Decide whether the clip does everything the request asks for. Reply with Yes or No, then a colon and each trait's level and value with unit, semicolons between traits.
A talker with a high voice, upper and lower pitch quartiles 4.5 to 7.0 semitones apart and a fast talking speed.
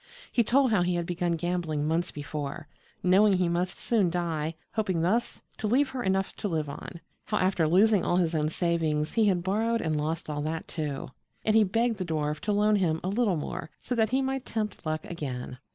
No: medium, 175 Hz; average, 5.1 semitones; fast, 215 wpm